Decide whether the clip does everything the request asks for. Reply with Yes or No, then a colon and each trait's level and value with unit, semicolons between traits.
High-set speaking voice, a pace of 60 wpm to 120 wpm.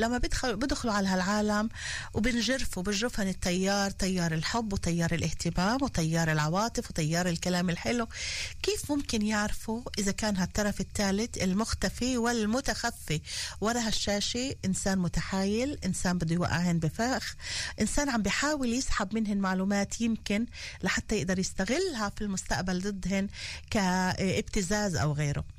Yes: high, 205 Hz; average, 115 wpm